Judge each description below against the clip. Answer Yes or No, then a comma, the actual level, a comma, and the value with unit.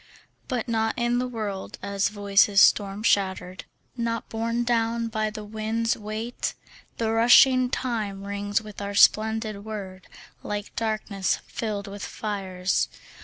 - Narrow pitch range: Yes, narrow, 2.3 semitones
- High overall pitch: Yes, high, 215 Hz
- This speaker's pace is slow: Yes, slow, 130 wpm